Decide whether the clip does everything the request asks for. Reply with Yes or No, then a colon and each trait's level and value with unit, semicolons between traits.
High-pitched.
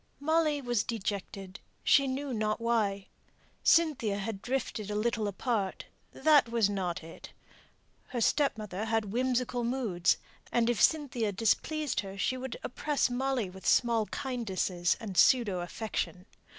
Yes: high, 230 Hz